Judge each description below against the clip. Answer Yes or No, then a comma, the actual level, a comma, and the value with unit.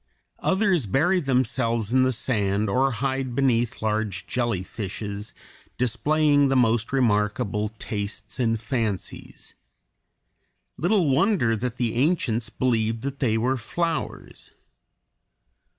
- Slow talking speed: Yes, slow, 105 wpm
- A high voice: No, low, 120 Hz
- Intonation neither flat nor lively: Yes, average, 3.8 semitones